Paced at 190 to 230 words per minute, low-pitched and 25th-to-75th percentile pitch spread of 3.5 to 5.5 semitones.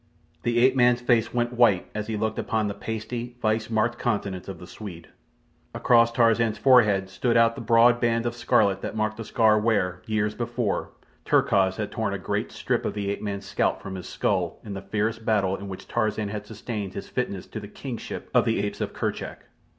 No: fast, 205 wpm; low, 110 Hz; average, 2.7 semitones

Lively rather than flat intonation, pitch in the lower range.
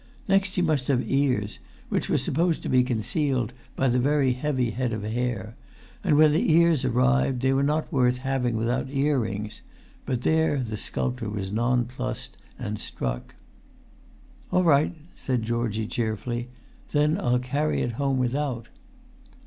No: average, 3.6 semitones; low, 125 Hz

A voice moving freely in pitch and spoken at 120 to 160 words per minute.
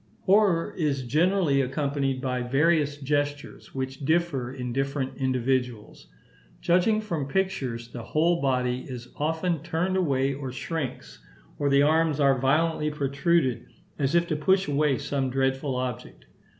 No: average, 3.7 semitones; slow, 135 wpm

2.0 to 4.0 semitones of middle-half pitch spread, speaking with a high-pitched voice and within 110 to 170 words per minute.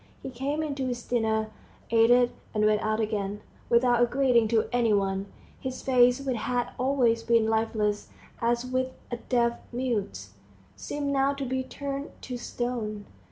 Yes: average, 2.8 semitones; high, 240 Hz; average, 165 wpm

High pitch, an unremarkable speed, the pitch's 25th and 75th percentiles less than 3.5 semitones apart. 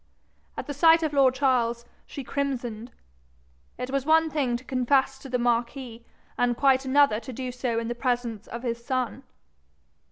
Yes: very high, 255 Hz; average, 170 wpm; narrow, 2.4 semitones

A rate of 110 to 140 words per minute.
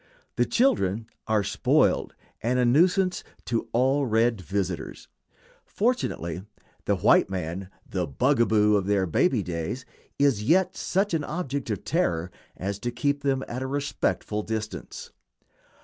Yes: slow, 135 wpm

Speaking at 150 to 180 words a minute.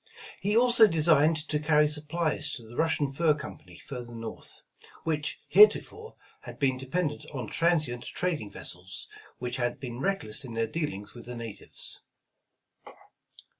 No: average, 140 wpm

